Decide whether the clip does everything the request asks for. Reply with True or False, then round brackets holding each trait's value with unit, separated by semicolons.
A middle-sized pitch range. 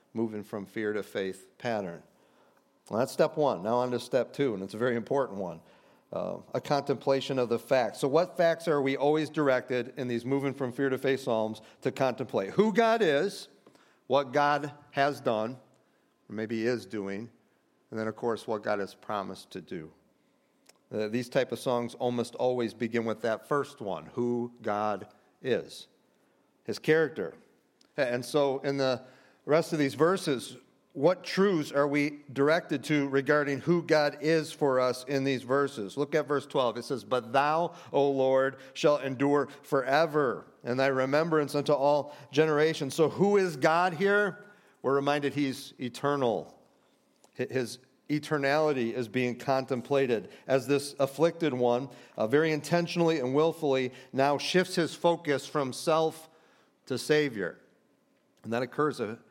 True (3.4 semitones)